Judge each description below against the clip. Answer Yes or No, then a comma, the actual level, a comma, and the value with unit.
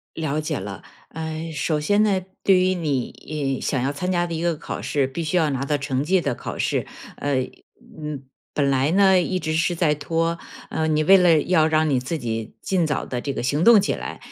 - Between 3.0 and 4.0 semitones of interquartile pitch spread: Yes, average, 3.7 semitones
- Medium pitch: Yes, medium, 155 Hz